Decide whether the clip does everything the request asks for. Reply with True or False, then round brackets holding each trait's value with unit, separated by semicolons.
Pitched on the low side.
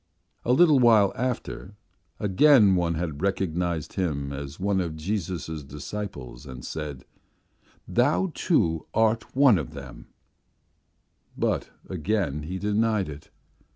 True (95 Hz)